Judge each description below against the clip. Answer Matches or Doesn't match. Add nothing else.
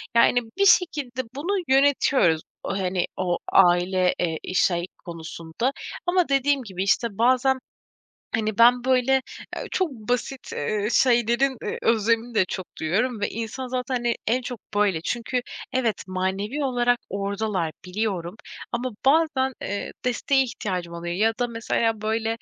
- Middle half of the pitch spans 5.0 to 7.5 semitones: Matches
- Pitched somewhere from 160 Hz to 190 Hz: Doesn't match